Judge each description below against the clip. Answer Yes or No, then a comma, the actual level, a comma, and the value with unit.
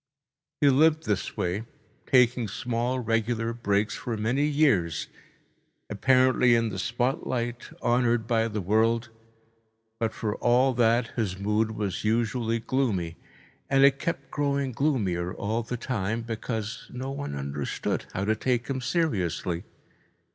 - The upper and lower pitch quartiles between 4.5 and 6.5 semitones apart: No, average, 3.3 semitones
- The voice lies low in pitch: Yes, low, 115 Hz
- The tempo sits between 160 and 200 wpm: No, slow, 135 wpm